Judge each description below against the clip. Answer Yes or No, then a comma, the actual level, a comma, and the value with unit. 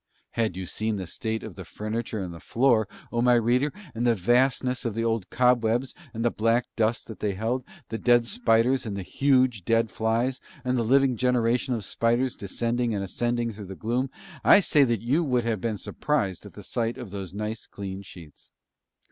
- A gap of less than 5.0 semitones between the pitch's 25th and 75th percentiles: Yes, narrow, 2.6 semitones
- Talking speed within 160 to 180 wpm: No, average, 200 wpm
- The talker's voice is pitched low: Yes, low, 115 Hz